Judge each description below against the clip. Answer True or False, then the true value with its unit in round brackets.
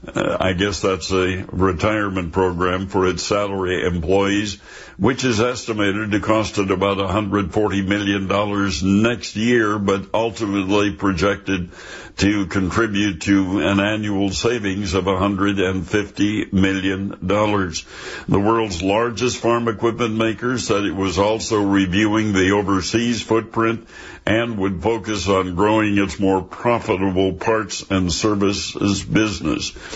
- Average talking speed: False (120 wpm)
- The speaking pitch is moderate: False (100 Hz)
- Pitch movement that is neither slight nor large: False (2.0 semitones)